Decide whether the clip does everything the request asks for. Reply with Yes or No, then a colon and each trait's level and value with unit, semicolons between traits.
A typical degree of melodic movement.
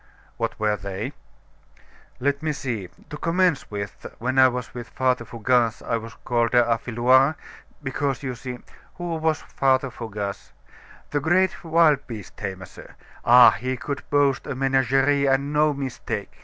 Yes: average, 3.4 semitones